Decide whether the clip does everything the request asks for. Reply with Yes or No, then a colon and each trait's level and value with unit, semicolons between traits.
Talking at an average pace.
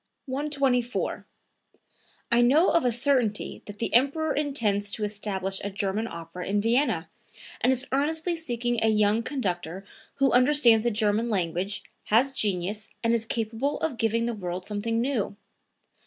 Yes: average, 150 wpm